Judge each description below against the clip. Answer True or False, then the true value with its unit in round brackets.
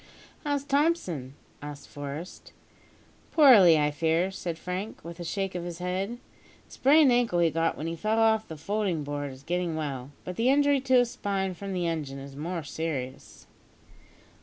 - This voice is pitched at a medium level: True (175 Hz)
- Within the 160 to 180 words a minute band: True (175 wpm)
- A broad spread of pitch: True (6.0 semitones)